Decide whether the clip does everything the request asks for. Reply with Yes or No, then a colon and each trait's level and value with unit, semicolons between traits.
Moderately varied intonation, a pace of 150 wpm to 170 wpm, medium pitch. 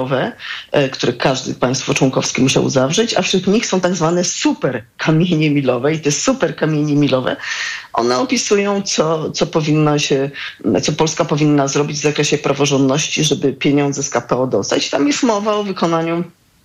Yes: average, 4.2 semitones; average, 155 wpm; medium, 150 Hz